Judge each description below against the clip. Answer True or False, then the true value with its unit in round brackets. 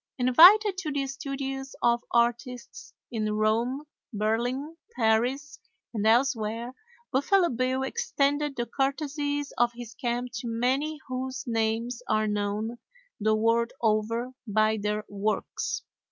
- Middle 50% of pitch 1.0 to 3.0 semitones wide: False (3.7 semitones)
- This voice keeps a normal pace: False (120 wpm)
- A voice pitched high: True (245 Hz)